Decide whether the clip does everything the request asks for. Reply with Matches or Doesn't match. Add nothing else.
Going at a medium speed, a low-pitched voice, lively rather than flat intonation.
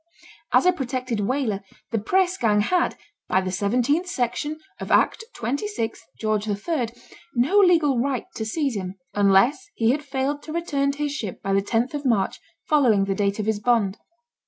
Doesn't match